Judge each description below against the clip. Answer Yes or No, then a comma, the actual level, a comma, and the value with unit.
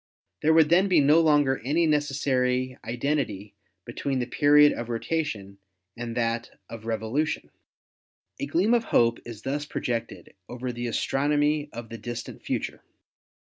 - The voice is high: No, low, 130 Hz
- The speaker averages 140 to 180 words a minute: Yes, average, 150 wpm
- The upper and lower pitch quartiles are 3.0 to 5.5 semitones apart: Yes, average, 4.1 semitones